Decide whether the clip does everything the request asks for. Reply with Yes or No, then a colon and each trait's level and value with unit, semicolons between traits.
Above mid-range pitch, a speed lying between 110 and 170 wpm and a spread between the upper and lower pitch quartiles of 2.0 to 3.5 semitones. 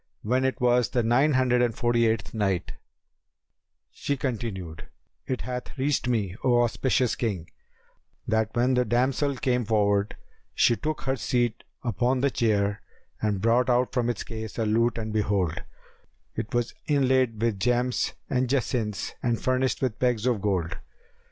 No: low, 120 Hz; average, 155 wpm; average, 2.8 semitones